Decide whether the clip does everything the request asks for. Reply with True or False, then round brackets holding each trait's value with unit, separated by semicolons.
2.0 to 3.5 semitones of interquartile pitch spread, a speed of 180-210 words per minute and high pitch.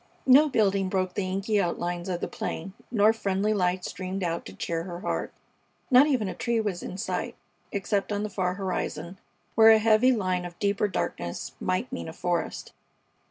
True (3.1 semitones; 185 wpm; 195 Hz)